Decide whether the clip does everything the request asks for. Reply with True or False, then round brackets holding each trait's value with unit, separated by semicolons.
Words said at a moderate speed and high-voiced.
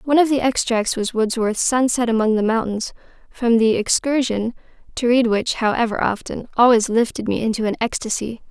True (170 wpm; 235 Hz)